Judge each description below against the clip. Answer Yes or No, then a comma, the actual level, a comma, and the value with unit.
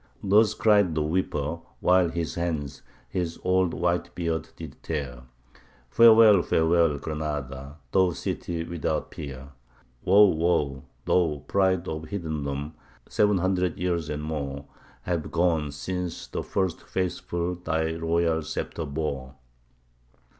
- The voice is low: Yes, very low, 85 Hz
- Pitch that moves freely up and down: No, average, 3.2 semitones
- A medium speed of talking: No, slow, 120 wpm